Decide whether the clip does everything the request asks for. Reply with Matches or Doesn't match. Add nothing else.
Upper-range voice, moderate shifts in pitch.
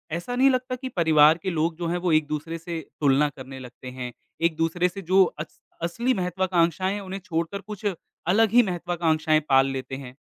Doesn't match